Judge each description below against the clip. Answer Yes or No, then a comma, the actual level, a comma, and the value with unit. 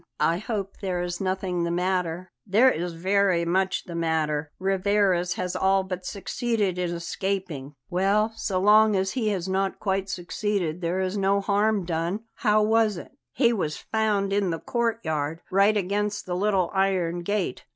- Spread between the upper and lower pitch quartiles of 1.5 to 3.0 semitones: Yes, narrow, 2.6 semitones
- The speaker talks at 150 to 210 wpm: Yes, average, 165 wpm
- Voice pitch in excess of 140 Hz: Yes, high, 190 Hz